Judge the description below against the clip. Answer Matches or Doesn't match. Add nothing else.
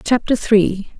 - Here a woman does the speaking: Matches